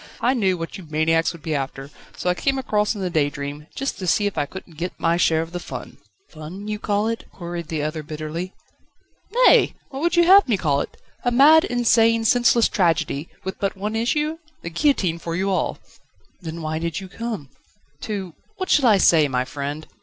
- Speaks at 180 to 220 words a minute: Yes, fast, 205 wpm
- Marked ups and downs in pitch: Yes, wide, 6.2 semitones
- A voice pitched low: No, medium, 180 Hz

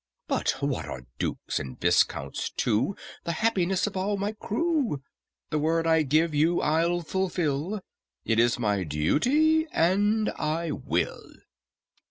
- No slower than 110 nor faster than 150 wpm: Yes, slow, 135 wpm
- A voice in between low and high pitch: Yes, medium, 165 Hz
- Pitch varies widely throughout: Yes, wide, 5.7 semitones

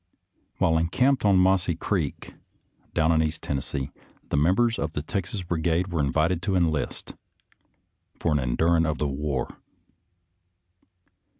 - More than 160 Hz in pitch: No, very low, 80 Hz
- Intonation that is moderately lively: Yes, average, 3.5 semitones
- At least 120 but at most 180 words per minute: Yes, average, 155 wpm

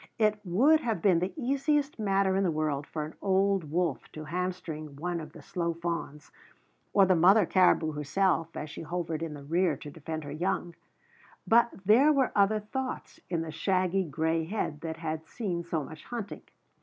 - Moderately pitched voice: Yes, medium, 175 Hz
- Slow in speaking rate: No, average, 185 wpm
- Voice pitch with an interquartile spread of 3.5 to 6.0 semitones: Yes, average, 3.9 semitones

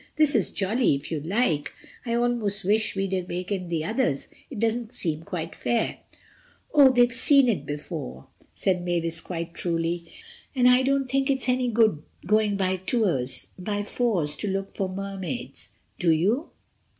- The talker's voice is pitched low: No, high, 195 Hz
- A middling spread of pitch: No, wide, 5.9 semitones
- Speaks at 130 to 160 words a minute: Yes, average, 150 wpm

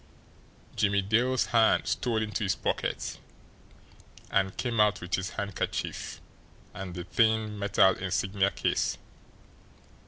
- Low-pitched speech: Yes, low, 100 Hz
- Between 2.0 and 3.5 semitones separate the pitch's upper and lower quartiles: Yes, narrow, 2.5 semitones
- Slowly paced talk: Yes, slow, 115 wpm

